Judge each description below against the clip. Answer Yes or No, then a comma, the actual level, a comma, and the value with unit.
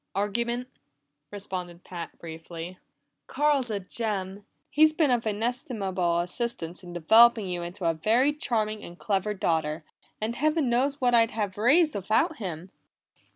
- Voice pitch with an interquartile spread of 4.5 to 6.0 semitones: Yes, average, 5.2 semitones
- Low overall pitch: No, high, 210 Hz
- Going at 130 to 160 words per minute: Yes, average, 140 wpm